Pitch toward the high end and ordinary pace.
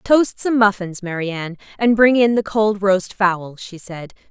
Yes: high, 200 Hz; average, 195 wpm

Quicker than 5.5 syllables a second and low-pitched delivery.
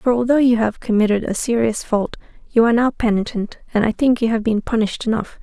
No: 6.0 syllables/s; high, 225 Hz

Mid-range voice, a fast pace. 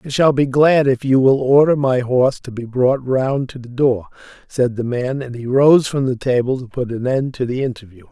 No: low, 130 Hz; fast, 245 wpm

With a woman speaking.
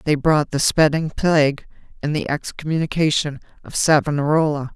Yes: female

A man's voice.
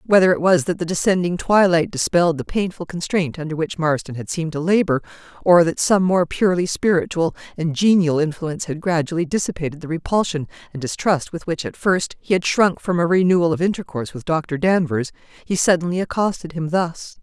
No: female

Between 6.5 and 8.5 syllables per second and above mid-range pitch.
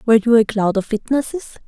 Yes: 6.9 syllables/s; high, 230 Hz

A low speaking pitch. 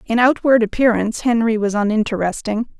No: high, 225 Hz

